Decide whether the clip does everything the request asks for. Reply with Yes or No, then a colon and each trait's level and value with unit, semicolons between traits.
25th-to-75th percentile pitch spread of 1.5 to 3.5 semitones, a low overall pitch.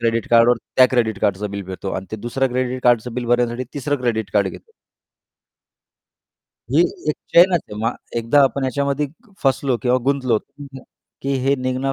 Yes: average, 2.9 semitones; low, 125 Hz